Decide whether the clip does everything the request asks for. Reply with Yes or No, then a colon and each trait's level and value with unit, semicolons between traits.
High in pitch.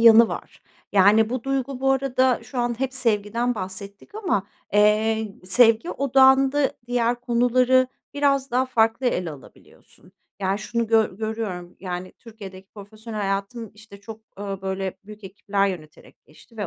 Yes: high, 220 Hz